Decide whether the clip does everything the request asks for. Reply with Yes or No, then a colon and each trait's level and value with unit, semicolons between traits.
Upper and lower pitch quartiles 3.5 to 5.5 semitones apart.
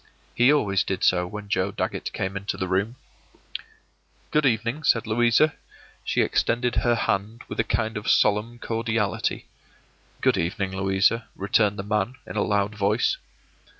No: average, 3.0 semitones